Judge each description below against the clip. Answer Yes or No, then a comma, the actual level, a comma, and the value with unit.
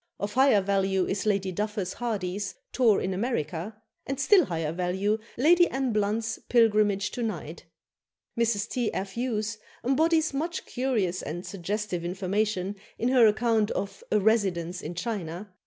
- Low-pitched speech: No, high, 210 Hz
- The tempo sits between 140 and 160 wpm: Yes, average, 145 wpm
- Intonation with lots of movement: No, average, 3.8 semitones